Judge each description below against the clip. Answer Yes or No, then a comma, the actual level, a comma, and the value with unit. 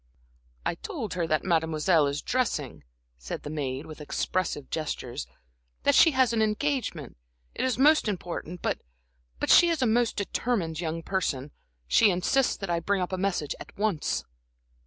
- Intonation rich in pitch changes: Yes, wide, 6.4 semitones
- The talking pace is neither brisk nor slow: Yes, average, 165 wpm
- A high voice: No, medium, 180 Hz